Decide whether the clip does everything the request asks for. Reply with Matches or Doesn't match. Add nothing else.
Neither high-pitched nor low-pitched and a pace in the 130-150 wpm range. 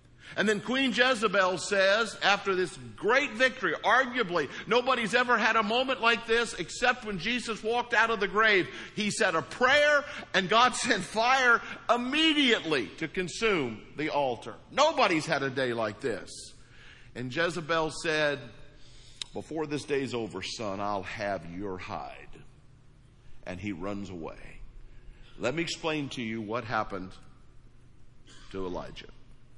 Matches